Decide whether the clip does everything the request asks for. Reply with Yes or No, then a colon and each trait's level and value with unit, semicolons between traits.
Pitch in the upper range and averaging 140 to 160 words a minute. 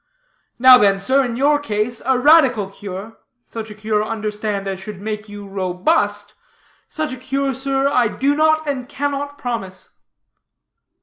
Yes: high, 230 Hz; average, 150 wpm